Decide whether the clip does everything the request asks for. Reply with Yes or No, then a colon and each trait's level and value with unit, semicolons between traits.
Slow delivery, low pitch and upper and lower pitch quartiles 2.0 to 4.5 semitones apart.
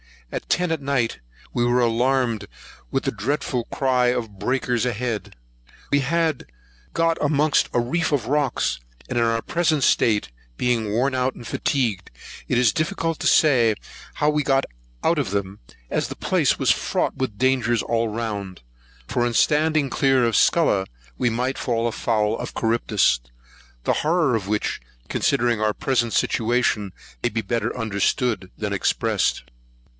No: average, 155 wpm; low, 120 Hz; average, 3.6 semitones